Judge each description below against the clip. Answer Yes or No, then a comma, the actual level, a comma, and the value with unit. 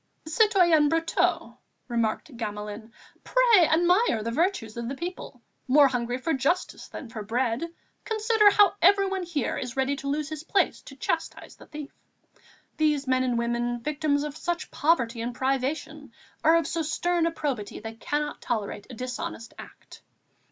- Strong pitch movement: Yes, wide, 5.7 semitones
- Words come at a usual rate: Yes, average, 160 wpm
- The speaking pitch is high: Yes, very high, 285 Hz